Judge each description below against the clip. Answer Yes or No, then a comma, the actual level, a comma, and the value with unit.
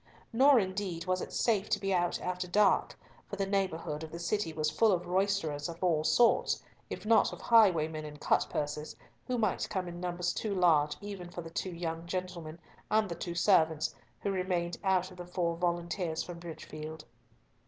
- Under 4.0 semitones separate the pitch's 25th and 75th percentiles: Yes, average, 3.0 semitones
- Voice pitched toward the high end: No, medium, 175 Hz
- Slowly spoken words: No, average, 185 wpm